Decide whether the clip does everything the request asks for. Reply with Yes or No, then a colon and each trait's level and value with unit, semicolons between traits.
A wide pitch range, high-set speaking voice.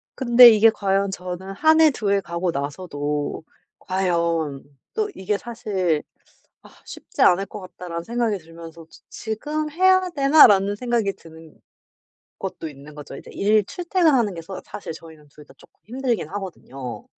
Yes: wide, 6.5 semitones; high, 195 Hz